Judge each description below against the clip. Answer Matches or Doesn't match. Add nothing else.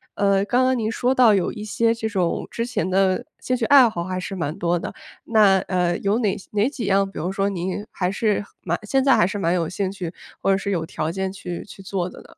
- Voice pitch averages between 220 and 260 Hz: Doesn't match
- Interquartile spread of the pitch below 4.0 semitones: Matches